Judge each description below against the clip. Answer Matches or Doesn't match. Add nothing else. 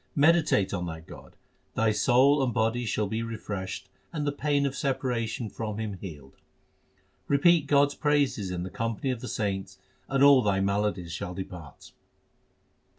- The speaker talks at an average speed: Matches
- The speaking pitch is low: Matches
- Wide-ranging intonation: Matches